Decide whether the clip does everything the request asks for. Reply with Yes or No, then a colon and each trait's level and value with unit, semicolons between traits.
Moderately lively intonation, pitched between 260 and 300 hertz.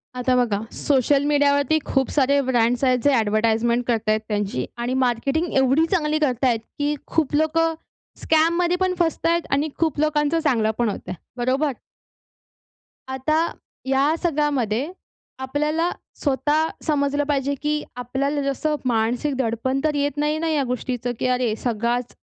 Yes: average, 3.7 semitones; very high, 275 Hz